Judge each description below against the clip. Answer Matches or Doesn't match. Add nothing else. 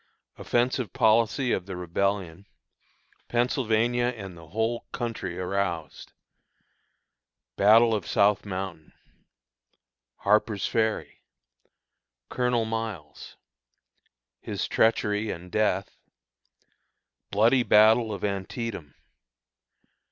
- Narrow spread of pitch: Doesn't match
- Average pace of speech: Doesn't match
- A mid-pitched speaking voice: Doesn't match